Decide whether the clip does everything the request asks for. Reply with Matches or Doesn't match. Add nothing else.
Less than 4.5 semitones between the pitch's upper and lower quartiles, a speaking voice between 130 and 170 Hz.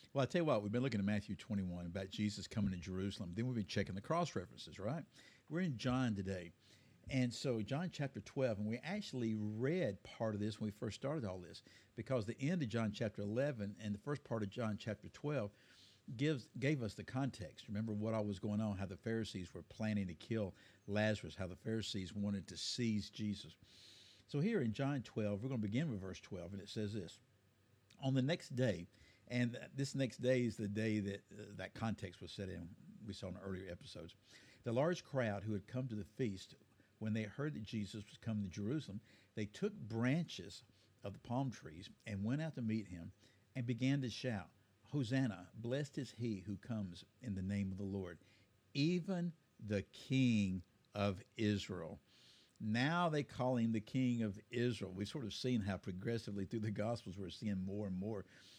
Doesn't match